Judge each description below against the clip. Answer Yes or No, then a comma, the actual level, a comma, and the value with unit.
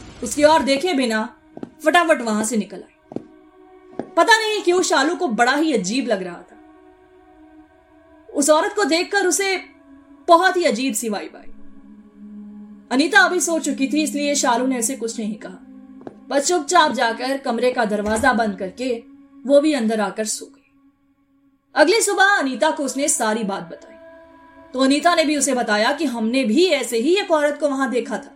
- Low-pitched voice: No, very high, 285 Hz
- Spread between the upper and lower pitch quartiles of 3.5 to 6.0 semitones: Yes, wide, 5.4 semitones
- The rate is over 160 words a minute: Yes, average, 170 wpm